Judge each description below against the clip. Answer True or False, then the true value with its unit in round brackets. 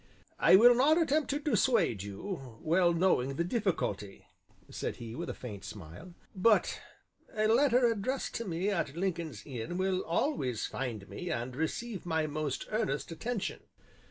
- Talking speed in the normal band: True (155 wpm)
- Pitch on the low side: False (175 Hz)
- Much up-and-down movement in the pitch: True (9.0 semitones)